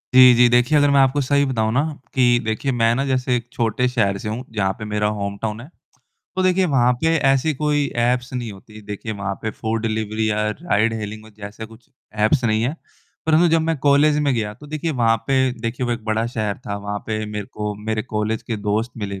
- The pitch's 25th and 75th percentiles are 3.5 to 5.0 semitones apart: Yes, average, 3.8 semitones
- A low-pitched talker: Yes, low, 115 Hz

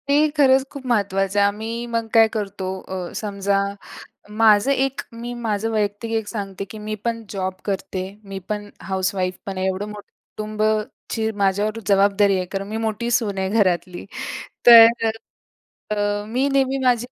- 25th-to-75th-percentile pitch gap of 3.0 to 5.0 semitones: No, narrow, 2.5 semitones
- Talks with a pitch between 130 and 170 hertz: No, high, 210 Hz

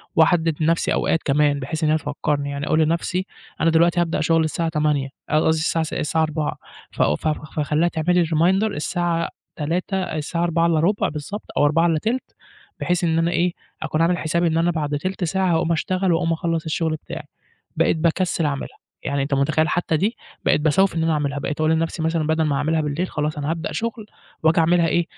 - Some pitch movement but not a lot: No, narrow, 2.1 semitones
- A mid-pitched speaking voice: Yes, medium, 160 Hz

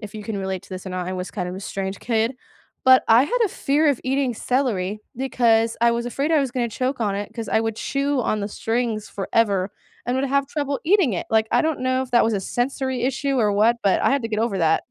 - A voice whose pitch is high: Yes, high, 235 Hz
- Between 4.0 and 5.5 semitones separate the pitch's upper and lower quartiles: Yes, average, 4.3 semitones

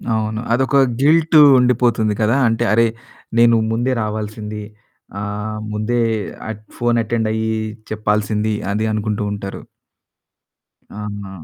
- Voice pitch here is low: Yes, low, 110 Hz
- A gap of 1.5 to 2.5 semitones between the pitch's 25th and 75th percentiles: Yes, narrow, 1.9 semitones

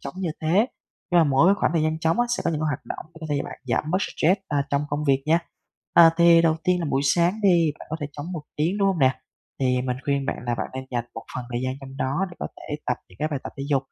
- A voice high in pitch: No, medium, 150 Hz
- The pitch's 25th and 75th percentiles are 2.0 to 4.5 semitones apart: Yes, average, 4.0 semitones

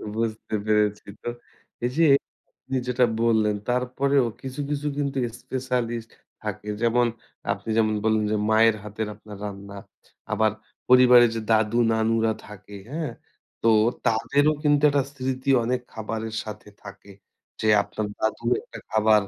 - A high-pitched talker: No, low, 115 Hz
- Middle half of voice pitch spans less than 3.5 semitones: Yes, average, 2.9 semitones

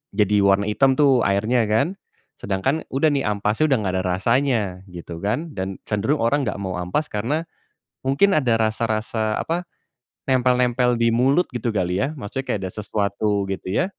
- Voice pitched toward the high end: No, low, 115 Hz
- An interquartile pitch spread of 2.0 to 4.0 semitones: No, average, 5.0 semitones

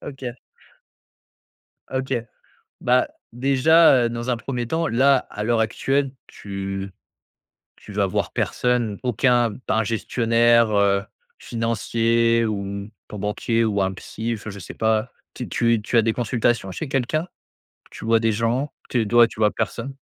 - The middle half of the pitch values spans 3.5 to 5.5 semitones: No, narrow, 2.6 semitones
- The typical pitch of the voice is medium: No, low, 115 Hz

